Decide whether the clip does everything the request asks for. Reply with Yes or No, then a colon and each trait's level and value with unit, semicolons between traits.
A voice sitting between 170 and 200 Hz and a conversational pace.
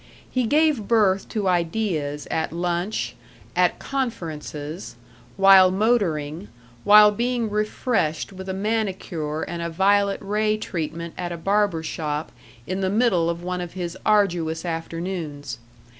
No: medium, 185 Hz; slow, 130 wpm